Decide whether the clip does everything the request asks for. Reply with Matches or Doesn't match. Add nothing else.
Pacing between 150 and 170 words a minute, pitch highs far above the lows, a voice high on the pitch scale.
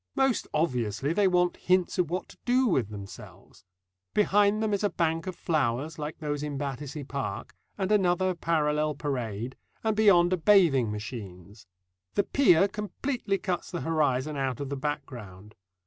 Doesn't match